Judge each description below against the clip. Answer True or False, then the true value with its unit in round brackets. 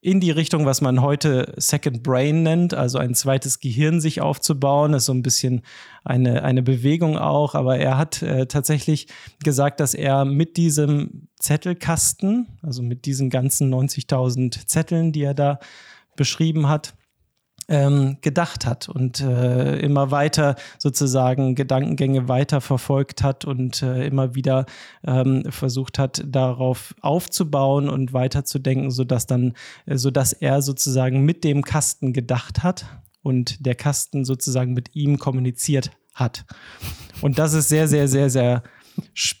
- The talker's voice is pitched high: False (135 Hz)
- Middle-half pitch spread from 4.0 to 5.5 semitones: False (2.4 semitones)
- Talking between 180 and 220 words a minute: False (140 wpm)